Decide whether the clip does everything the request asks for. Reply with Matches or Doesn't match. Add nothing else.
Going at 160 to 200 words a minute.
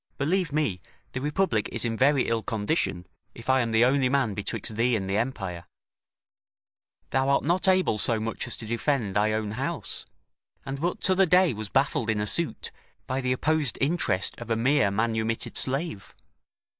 Matches